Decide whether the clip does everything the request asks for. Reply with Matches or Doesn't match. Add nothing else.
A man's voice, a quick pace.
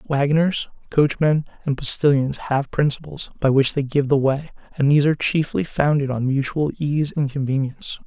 Doesn't match